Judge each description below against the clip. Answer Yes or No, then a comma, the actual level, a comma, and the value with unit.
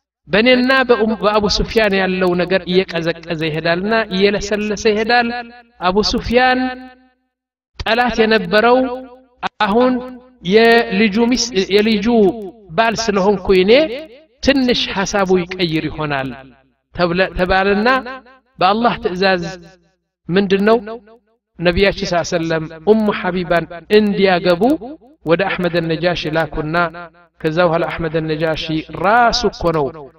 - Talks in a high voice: Yes, high, 200 Hz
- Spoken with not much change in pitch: No, average, 5.1 semitones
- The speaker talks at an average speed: Yes, average, 80 wpm